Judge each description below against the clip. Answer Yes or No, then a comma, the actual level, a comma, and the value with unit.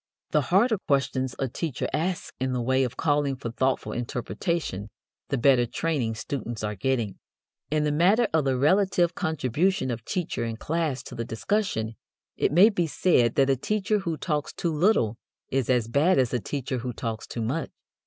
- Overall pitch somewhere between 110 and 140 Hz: Yes, low, 135 Hz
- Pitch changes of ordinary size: No, wide, 5.7 semitones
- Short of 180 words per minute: No, average, 185 wpm